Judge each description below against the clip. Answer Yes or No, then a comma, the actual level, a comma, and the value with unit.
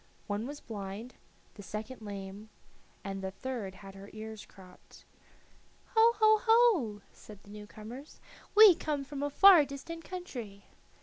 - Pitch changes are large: Yes, wide, 7.0 semitones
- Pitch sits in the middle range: No, high, 225 Hz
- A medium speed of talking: Yes, average, 145 wpm